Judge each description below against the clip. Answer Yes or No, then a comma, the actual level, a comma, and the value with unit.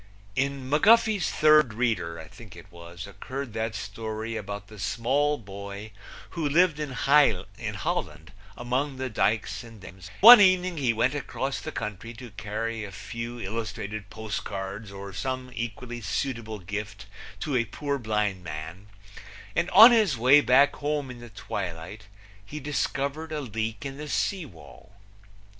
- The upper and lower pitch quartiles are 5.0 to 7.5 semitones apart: Yes, wide, 5.5 semitones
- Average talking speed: Yes, average, 155 wpm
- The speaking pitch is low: Yes, low, 115 Hz